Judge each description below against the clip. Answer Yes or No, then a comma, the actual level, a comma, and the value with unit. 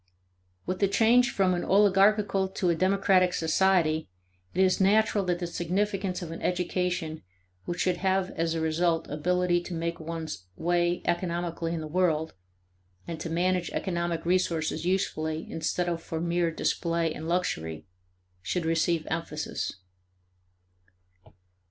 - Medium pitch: Yes, medium, 175 Hz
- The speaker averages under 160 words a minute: Yes, average, 140 wpm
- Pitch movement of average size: No, narrow, 2.2 semitones